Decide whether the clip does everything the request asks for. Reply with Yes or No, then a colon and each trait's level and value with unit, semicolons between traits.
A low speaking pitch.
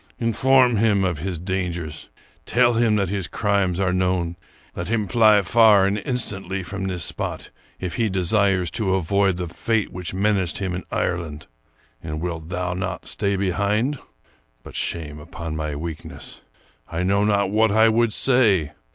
Yes: very low, 95 Hz